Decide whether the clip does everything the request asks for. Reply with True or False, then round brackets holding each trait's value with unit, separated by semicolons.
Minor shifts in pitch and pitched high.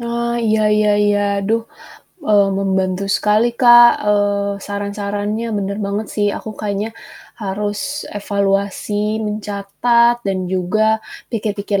True (1.3 semitones; 205 Hz)